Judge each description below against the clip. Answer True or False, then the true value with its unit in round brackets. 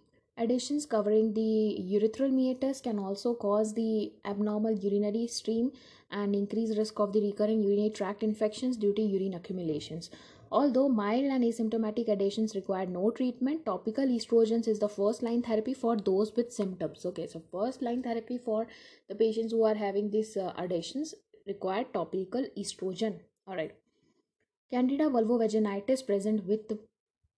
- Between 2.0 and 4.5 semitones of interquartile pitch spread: True (2.7 semitones)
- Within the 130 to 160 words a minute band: True (140 wpm)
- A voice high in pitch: True (220 Hz)